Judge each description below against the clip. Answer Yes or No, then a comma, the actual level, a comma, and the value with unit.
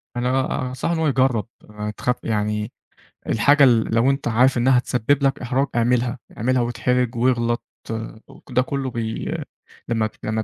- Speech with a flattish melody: Yes, narrow, 2.1 semitones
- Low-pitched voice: Yes, low, 125 Hz